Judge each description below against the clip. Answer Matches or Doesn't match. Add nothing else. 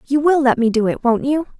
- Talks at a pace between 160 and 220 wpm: Doesn't match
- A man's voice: Doesn't match